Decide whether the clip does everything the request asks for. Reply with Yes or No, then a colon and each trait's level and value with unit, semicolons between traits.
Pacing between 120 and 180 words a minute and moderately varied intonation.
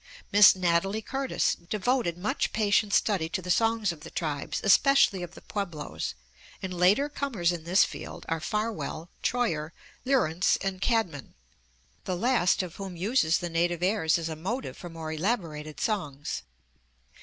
Yes: average, 155 wpm; average, 4.6 semitones